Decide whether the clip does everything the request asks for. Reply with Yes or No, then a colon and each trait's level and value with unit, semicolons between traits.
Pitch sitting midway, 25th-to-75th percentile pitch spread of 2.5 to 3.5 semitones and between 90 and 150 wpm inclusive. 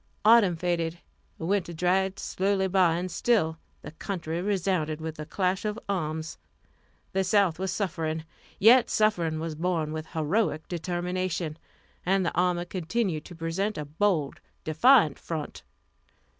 Yes: medium, 175 Hz; average, 3.2 semitones; slow, 135 wpm